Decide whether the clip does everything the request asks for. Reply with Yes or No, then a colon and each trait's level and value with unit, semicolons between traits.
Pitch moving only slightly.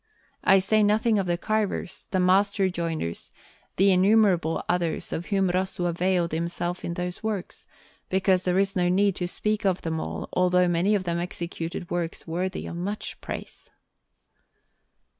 Yes: narrow, 2.2 semitones